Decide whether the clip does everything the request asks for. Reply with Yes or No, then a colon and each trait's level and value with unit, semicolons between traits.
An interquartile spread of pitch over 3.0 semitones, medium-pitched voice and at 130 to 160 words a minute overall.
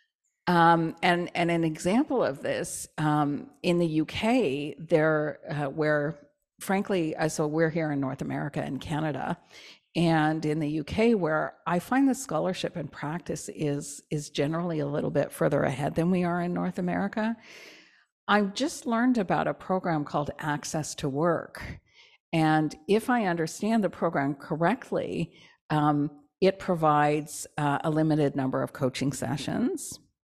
Yes: average, 3.6 semitones; medium, 160 Hz; average, 150 wpm